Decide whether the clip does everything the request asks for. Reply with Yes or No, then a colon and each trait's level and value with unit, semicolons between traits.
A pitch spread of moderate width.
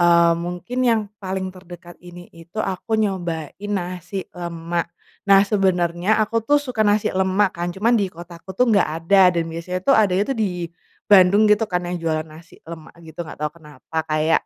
Yes: average, 3.2 semitones